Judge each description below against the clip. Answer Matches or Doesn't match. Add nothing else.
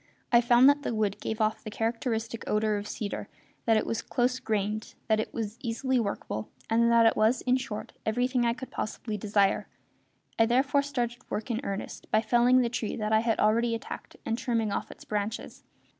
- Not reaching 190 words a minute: Doesn't match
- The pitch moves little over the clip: Matches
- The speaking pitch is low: Doesn't match